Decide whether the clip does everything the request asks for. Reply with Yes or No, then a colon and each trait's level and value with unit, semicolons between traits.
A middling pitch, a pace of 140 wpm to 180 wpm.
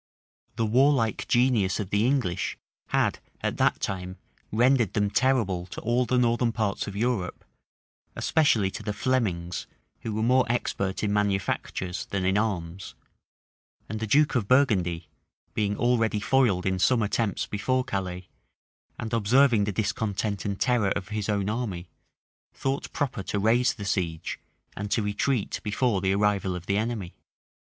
No: low, 105 Hz; average, 155 wpm